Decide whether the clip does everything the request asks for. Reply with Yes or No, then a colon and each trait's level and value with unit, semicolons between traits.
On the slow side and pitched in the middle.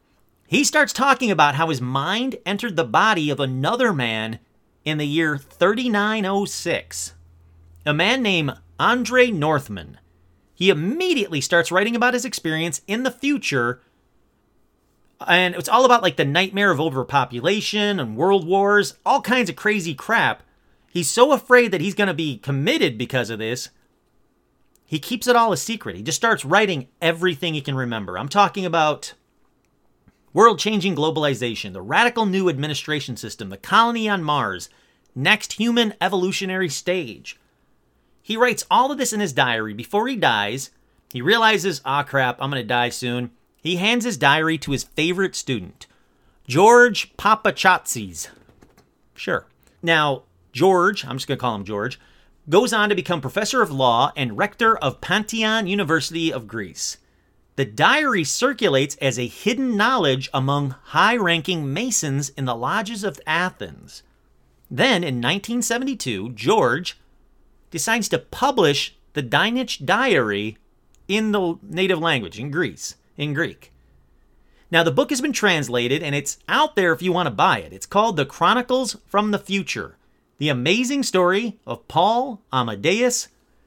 No: average, 150 wpm; medium, 170 Hz